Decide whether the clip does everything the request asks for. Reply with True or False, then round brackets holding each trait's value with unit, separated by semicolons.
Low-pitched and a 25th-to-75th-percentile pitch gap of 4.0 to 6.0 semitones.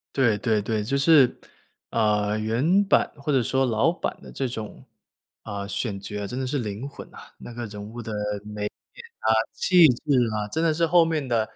True (115 Hz; 4.8 semitones)